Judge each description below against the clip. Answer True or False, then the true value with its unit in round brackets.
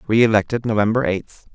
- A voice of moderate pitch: False (110 Hz)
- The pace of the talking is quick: False (115 wpm)